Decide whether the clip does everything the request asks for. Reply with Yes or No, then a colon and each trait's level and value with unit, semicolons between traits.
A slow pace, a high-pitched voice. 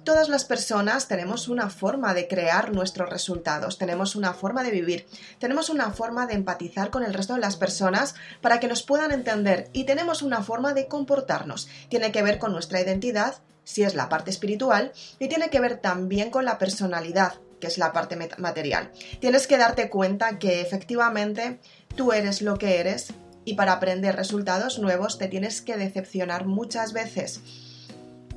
No: average, 175 wpm; high, 205 Hz